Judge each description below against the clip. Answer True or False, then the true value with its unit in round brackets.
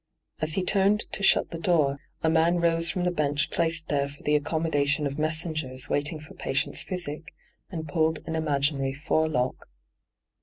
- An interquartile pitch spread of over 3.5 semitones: False (2.5 semitones)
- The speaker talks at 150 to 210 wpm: True (175 wpm)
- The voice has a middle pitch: True (155 Hz)